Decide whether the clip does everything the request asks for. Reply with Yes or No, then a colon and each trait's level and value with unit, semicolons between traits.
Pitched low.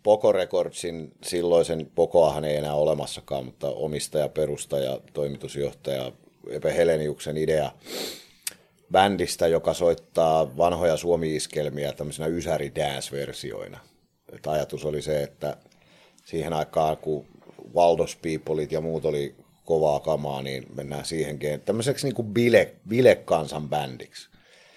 Yes: very low, 75 Hz